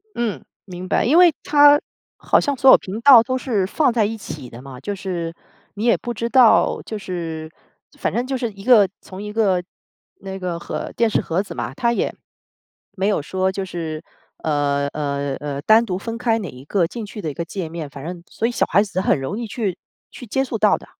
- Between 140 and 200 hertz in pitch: Yes, high, 195 Hz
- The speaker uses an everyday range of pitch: No, wide, 5.7 semitones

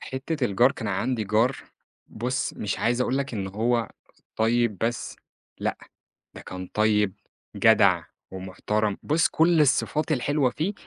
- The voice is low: Yes, low, 120 Hz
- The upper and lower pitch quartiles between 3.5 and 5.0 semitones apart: Yes, average, 4.2 semitones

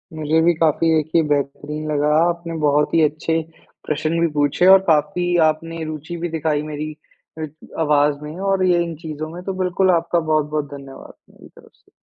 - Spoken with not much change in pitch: Yes, narrow, 2.2 semitones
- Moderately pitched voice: Yes, medium, 155 Hz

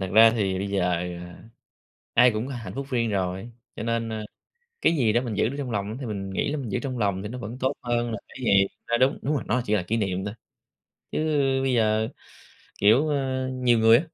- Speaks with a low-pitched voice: Yes, low, 115 Hz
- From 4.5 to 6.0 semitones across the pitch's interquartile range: No, average, 4.0 semitones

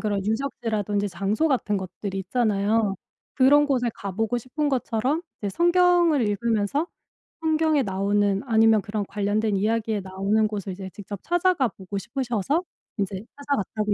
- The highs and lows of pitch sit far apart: No, average, 4.9 semitones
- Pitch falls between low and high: No, high, 220 Hz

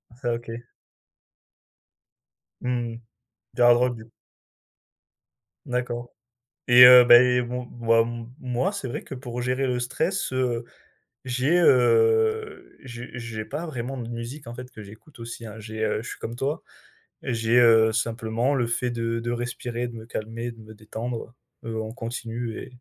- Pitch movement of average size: No, narrow, 1.6 semitones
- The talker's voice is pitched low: Yes, low, 120 Hz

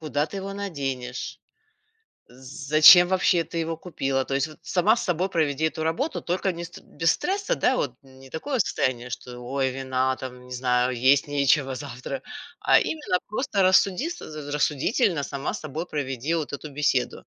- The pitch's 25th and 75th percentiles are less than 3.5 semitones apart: No, average, 5.2 semitones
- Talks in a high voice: No, medium, 150 Hz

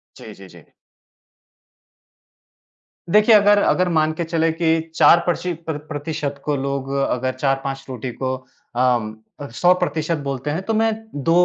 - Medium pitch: Yes, medium, 150 Hz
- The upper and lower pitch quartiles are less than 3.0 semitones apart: No, average, 3.8 semitones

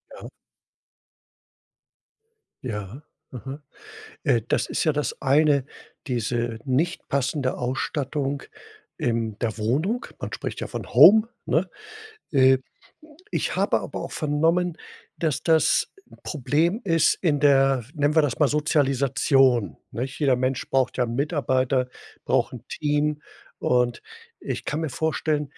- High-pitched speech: No, medium, 140 Hz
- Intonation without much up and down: No, average, 3.1 semitones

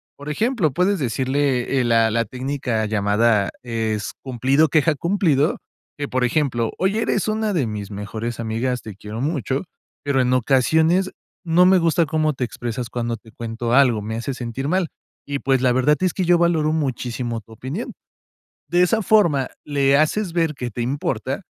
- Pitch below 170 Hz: Yes, low, 135 Hz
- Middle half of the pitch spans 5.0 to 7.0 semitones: Yes, average, 5.3 semitones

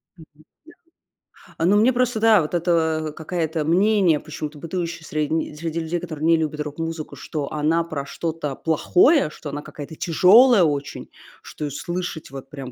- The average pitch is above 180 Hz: No, medium, 160 Hz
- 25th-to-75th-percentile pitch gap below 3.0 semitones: Yes, narrow, 2.6 semitones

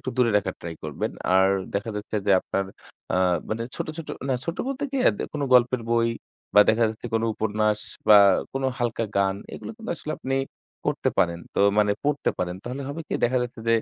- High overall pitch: No, low, 115 Hz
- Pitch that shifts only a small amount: No, average, 4.4 semitones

